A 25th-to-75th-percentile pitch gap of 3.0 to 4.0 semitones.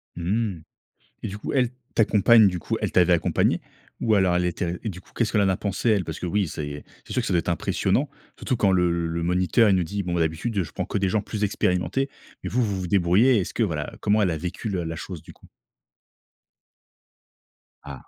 Yes: average, 3.6 semitones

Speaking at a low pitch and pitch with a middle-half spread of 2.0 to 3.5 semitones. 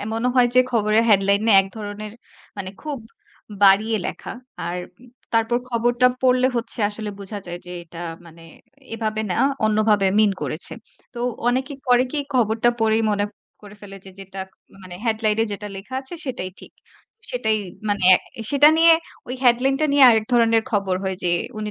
No: high, 220 Hz; average, 3.2 semitones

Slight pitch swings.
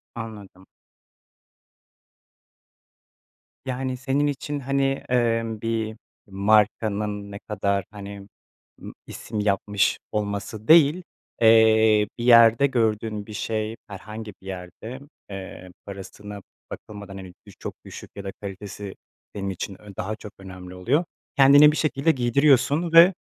No: average, 3.7 semitones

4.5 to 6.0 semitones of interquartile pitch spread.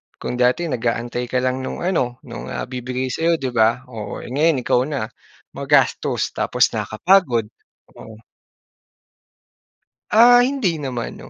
Yes: average, 5.3 semitones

